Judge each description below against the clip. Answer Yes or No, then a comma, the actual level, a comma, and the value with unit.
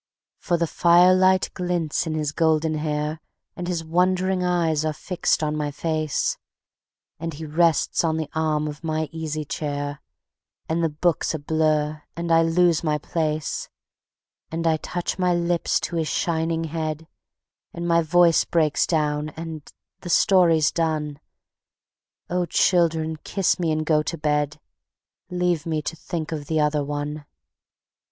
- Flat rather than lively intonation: Yes, narrow, 2.0 semitones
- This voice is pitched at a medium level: Yes, medium, 160 Hz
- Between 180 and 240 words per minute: No, average, 150 wpm